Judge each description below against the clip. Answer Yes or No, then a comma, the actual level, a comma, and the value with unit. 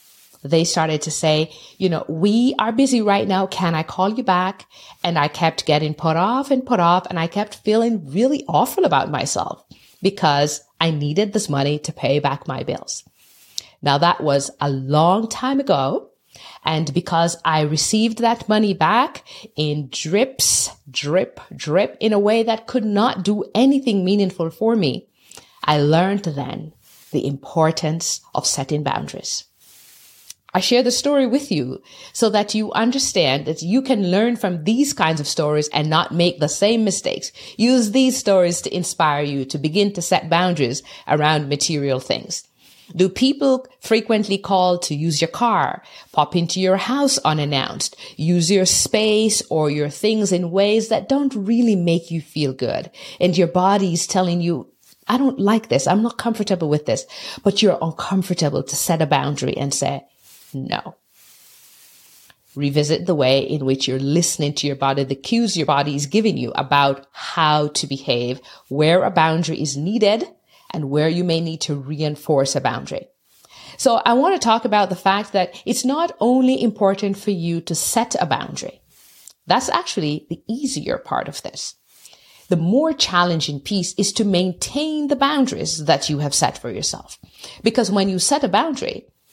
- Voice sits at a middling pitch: Yes, medium, 175 Hz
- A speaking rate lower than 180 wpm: Yes, average, 170 wpm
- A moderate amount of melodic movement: No, wide, 6.2 semitones